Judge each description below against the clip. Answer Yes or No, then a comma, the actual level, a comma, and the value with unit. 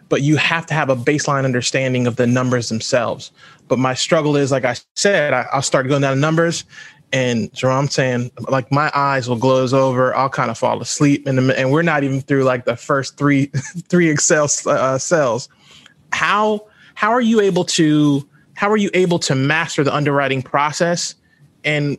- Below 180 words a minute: No, average, 195 wpm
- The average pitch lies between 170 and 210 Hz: No, medium, 140 Hz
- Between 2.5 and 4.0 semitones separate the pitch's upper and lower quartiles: Yes, average, 3.1 semitones